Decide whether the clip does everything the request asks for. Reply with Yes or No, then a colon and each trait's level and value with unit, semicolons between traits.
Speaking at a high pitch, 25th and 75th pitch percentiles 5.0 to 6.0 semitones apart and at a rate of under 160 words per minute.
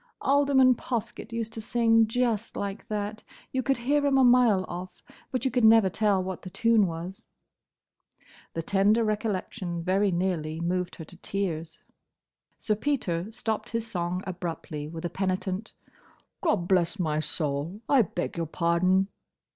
No: high, 195 Hz; average, 4.6 semitones; average, 145 wpm